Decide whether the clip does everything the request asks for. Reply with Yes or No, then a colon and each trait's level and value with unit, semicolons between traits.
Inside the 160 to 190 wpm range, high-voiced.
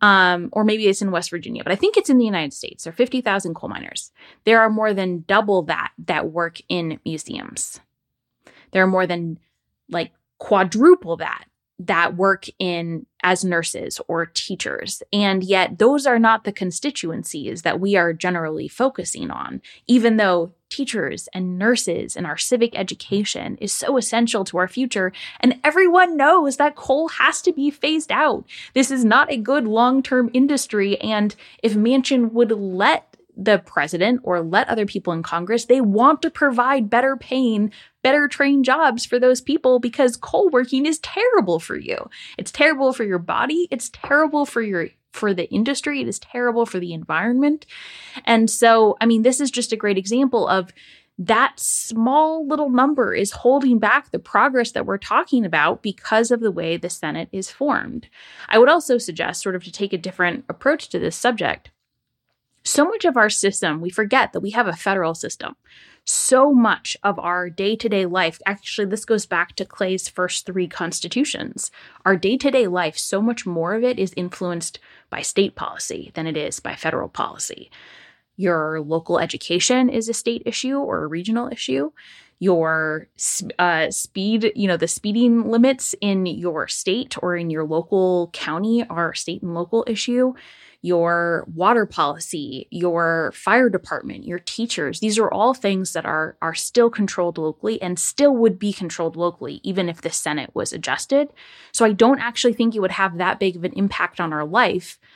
Yes: average, 180 wpm; high, 210 Hz